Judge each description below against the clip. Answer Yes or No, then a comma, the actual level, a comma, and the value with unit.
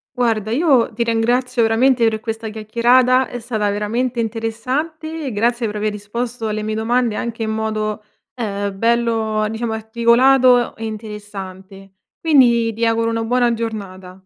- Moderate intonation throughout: No, narrow, 2.1 semitones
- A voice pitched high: Yes, high, 225 Hz